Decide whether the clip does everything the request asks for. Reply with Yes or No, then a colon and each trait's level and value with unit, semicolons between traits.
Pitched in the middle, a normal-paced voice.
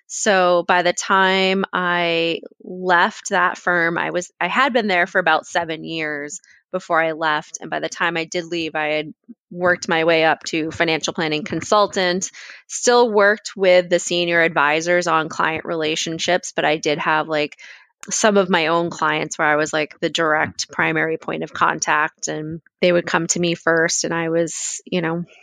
Yes: medium, 170 Hz; average, 185 wpm